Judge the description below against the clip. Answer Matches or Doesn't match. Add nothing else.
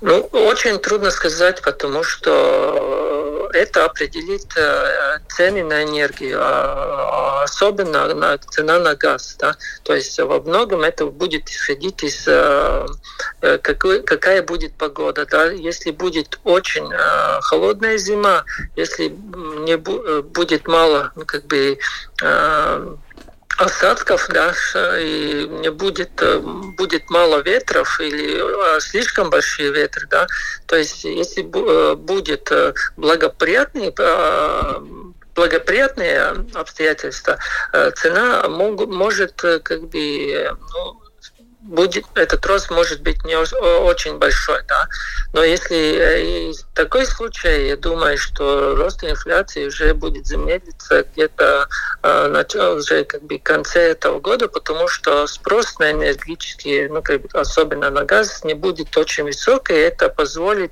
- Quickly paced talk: Doesn't match